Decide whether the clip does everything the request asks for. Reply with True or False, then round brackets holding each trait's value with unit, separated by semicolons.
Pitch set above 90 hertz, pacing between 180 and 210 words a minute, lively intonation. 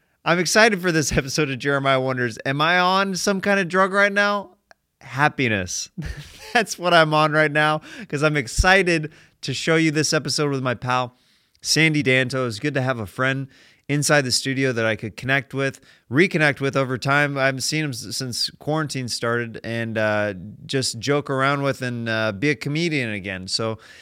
False (140 Hz; 190 wpm; 3.7 semitones)